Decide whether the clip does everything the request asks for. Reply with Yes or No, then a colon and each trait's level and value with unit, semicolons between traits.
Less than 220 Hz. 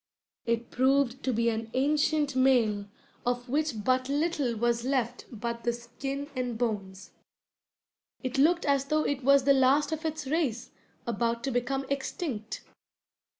No: very high, 255 Hz